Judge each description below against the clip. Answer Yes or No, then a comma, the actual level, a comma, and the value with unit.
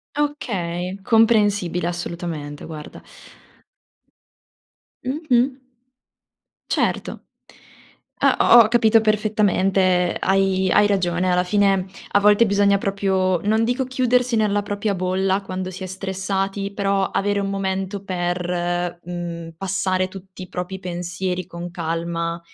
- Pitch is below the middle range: No, high, 190 Hz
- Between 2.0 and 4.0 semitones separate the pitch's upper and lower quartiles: Yes, narrow, 2.4 semitones